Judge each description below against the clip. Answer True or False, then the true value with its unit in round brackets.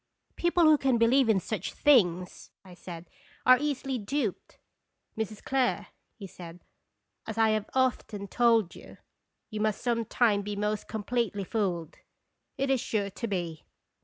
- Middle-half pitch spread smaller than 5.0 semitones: True (4.0 semitones)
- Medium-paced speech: True (160 wpm)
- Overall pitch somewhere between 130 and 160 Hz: False (220 Hz)